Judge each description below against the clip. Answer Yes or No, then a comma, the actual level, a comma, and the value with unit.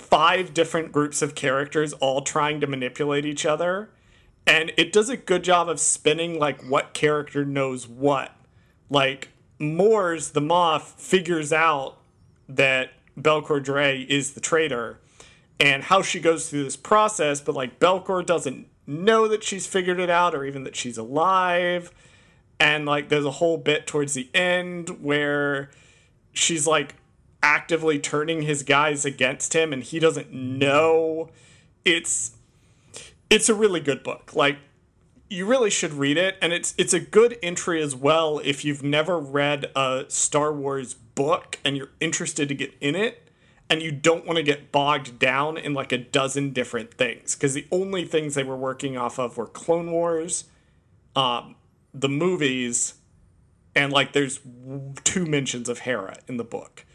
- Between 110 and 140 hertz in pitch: No, medium, 150 Hz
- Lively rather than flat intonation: No, average, 3.3 semitones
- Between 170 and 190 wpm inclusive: No, average, 160 wpm